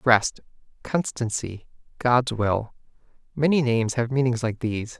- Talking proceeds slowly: Yes, slow, 120 wpm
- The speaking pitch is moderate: No, low, 120 Hz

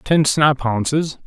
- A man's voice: Yes, male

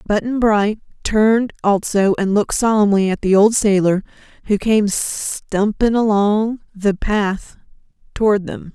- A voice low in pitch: No, high, 205 Hz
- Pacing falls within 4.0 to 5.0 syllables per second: Yes, 4.1 syllables/s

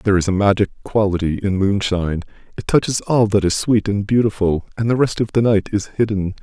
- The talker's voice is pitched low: Yes, low, 100 Hz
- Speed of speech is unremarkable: No, fast, 215 wpm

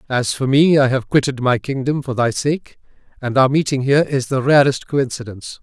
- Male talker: Yes, male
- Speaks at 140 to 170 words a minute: No, fast, 205 wpm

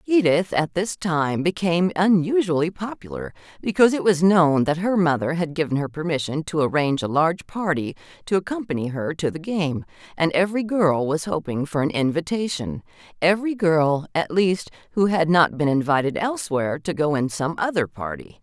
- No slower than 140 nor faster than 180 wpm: Yes, average, 170 wpm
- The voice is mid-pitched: Yes, medium, 165 Hz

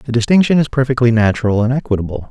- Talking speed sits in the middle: Yes, average, 180 wpm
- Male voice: Yes, male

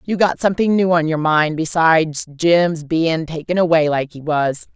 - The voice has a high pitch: No, medium, 165 Hz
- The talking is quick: No, average, 190 wpm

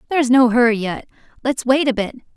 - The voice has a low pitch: No, high, 245 Hz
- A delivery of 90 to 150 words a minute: No, fast, 205 wpm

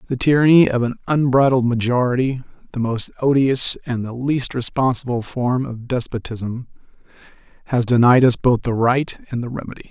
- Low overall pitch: Yes, low, 125 Hz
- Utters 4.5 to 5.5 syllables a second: Yes, 5.2 syllables/s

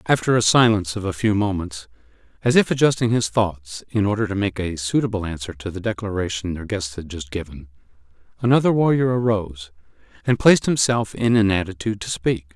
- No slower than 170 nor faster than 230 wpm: Yes, average, 180 wpm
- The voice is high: No, low, 100 Hz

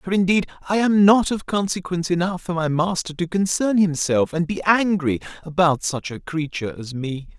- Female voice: No, male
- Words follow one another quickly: No, average, 185 wpm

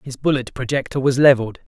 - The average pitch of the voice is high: No, low, 130 Hz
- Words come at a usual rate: Yes, average, 170 wpm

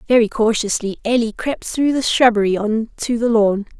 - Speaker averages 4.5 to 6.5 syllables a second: Yes, 5.0 syllables/s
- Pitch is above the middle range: Yes, high, 225 Hz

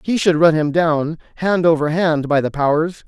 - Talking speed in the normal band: No, fast, 215 wpm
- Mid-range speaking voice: Yes, medium, 160 Hz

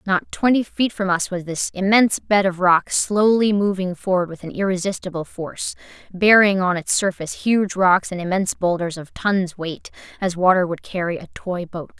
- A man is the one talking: No, female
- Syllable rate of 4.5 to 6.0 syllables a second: Yes, 5.0 syllables/s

